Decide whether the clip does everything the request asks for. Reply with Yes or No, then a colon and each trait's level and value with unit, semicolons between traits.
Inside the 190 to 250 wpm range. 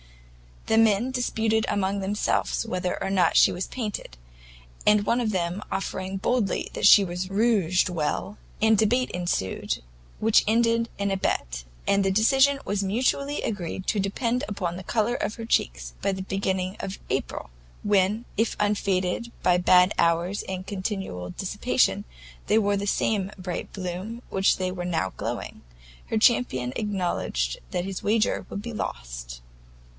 No: average, 155 wpm